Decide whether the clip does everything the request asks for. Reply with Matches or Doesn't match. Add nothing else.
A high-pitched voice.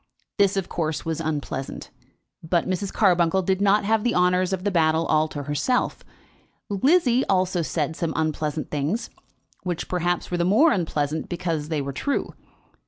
Doesn't match